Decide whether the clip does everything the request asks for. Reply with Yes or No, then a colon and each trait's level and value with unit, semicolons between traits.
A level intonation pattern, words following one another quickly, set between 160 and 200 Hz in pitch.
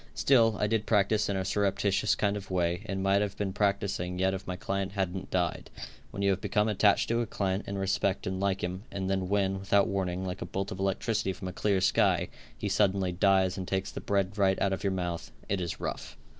No: narrow, 1.3 semitones; fast, 235 wpm; very low, 95 Hz